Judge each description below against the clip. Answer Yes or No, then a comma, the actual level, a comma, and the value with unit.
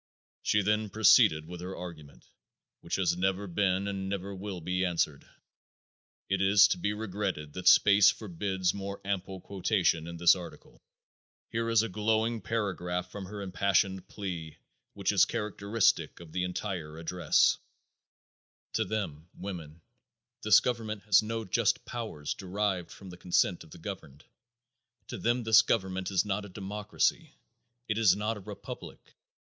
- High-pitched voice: No, very low, 95 Hz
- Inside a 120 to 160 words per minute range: Yes, average, 150 wpm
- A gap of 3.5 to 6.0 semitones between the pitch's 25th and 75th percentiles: No, average, 2.8 semitones